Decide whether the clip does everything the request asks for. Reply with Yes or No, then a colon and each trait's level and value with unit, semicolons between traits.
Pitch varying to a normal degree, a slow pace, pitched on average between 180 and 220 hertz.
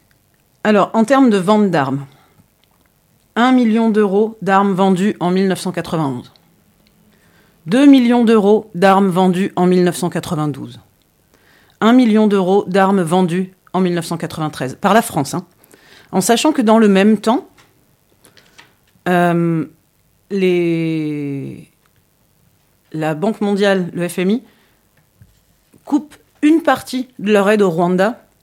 Yes: average, 4.0 semitones; slow, 110 wpm; high, 190 Hz